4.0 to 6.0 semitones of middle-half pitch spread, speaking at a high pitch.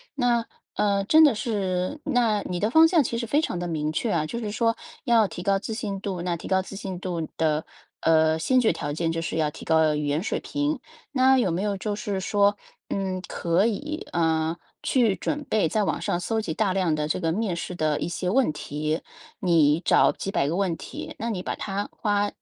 Yes: average, 5.3 semitones; high, 195 Hz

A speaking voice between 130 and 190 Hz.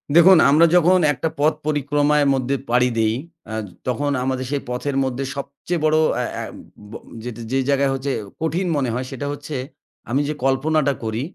Yes: medium, 140 Hz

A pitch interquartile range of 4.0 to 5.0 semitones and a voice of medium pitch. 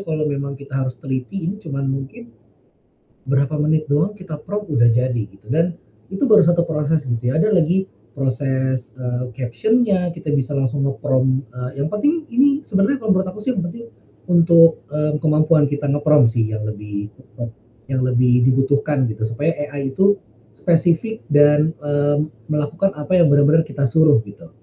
Yes: average, 4.3 semitones; medium, 145 Hz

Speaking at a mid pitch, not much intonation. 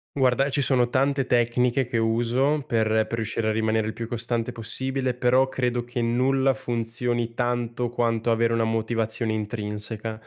No: low, 120 Hz; narrow, 2.0 semitones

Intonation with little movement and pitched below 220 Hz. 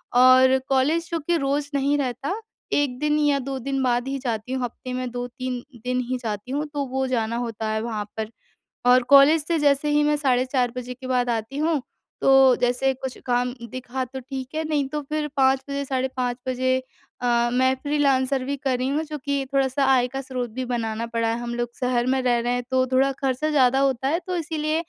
No: narrow, 2.2 semitones; very high, 260 Hz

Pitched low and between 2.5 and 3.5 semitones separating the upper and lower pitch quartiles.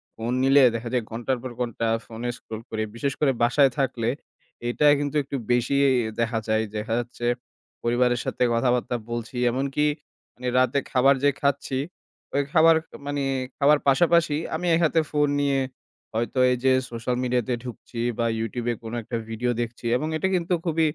Yes: low, 125 Hz; average, 3.1 semitones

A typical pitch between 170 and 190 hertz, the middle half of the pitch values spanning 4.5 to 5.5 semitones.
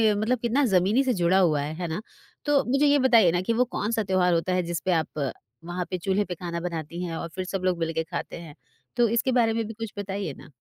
Yes: medium, 185 Hz; average, 4.9 semitones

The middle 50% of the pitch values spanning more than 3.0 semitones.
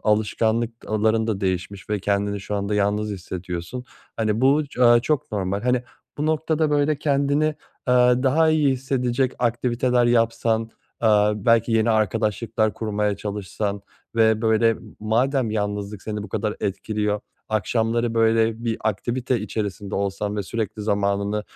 No: average, 2.7 semitones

